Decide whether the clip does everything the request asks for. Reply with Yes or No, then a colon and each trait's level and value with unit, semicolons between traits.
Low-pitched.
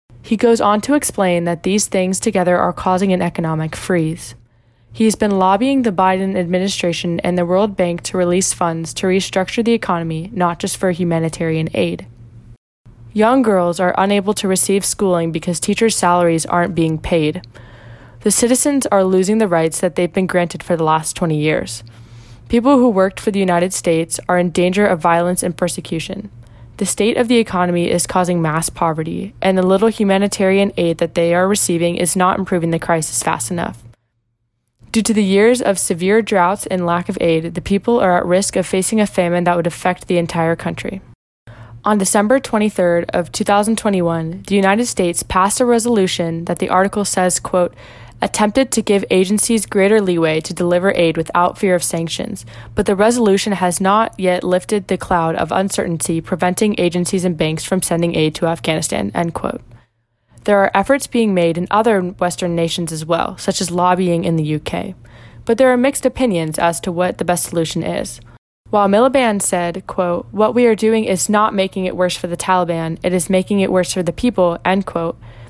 No: medium, 180 Hz